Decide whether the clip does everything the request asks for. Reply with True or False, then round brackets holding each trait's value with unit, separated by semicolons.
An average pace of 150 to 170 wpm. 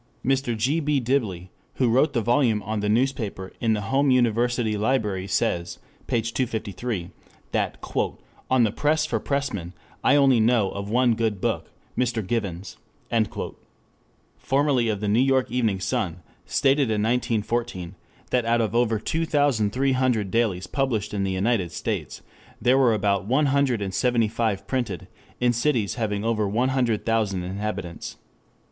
True (155 wpm)